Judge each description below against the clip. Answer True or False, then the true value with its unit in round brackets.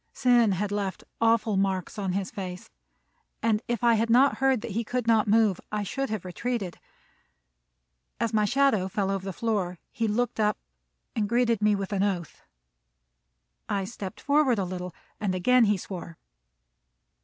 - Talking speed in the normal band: True (165 wpm)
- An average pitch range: True (3.2 semitones)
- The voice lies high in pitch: True (210 Hz)